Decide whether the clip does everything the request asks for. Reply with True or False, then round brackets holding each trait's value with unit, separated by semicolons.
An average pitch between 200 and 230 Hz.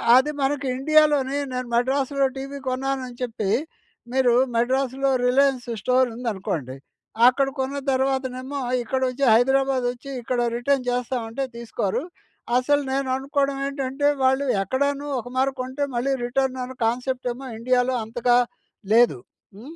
False (260 Hz)